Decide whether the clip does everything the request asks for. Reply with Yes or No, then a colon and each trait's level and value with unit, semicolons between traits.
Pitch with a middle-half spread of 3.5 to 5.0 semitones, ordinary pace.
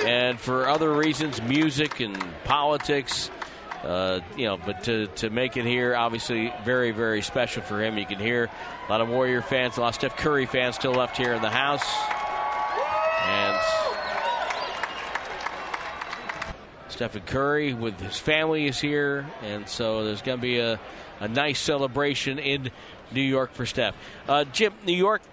Yes: average, 3.9 semitones; average, 165 wpm